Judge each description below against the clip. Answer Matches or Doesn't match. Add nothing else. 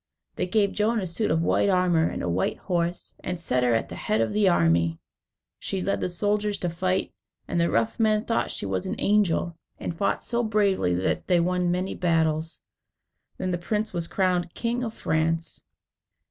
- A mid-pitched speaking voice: Matches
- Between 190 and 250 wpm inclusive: Matches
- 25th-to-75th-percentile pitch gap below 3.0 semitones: Doesn't match